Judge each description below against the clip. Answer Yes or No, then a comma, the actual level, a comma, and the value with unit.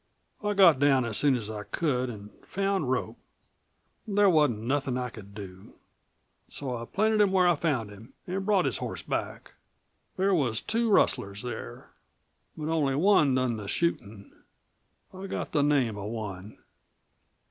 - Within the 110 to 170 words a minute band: Yes, average, 160 wpm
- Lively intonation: Yes, wide, 8.5 semitones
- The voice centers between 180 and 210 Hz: No, low, 135 Hz